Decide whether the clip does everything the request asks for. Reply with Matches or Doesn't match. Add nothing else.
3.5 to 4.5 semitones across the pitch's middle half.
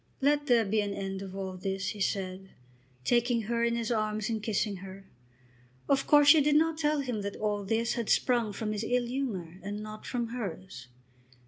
Matches